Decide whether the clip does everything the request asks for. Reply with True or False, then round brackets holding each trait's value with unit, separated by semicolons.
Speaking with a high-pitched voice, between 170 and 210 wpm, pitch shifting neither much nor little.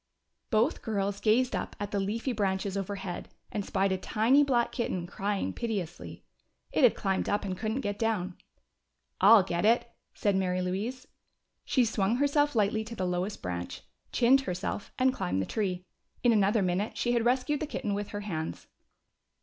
True (205 Hz; 175 wpm; 3.7 semitones)